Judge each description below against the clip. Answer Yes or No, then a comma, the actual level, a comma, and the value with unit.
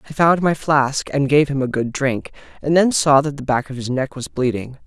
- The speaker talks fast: Yes, fast, 260 wpm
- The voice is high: No, low, 135 Hz